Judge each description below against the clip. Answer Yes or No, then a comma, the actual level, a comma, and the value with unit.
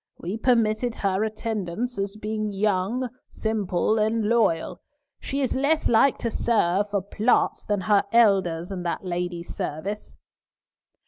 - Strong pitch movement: No, average, 3.3 semitones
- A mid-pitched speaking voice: No, high, 210 Hz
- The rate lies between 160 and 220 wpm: No, slow, 135 wpm